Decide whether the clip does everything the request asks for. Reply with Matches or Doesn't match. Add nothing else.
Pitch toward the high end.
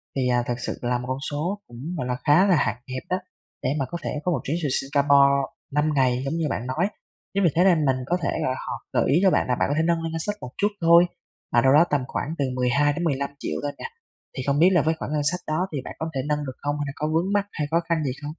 Doesn't match